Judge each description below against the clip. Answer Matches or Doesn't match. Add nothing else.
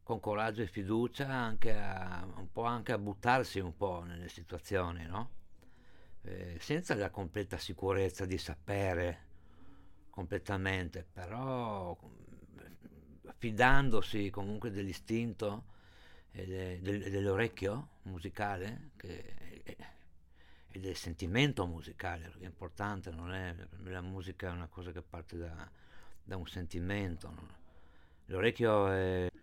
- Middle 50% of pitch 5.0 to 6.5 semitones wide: Doesn't match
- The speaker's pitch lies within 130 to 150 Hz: Doesn't match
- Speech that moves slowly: Matches